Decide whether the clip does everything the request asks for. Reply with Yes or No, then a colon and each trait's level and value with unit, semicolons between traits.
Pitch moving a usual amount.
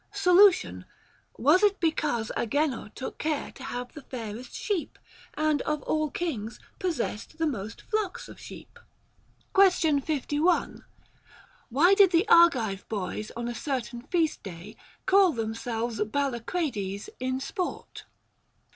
No: wide, 6.7 semitones